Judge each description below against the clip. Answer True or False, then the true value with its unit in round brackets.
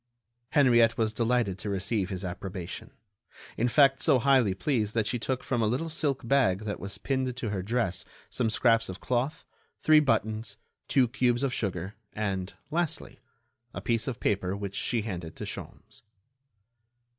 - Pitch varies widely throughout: False (4.4 semitones)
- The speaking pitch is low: True (115 Hz)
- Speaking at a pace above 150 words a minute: True (165 wpm)